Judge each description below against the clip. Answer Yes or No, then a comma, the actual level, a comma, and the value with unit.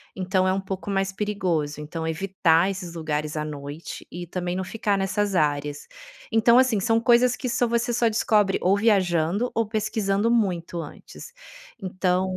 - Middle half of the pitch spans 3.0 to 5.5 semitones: Yes, average, 4.2 semitones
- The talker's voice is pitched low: No, high, 190 Hz